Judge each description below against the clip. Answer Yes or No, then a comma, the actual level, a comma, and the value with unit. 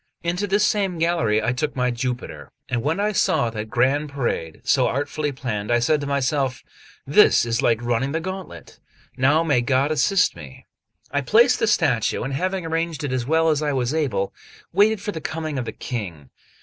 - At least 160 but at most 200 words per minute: Yes, average, 195 wpm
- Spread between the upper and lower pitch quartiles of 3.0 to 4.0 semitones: No, average, 5.3 semitones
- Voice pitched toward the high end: No, medium, 140 Hz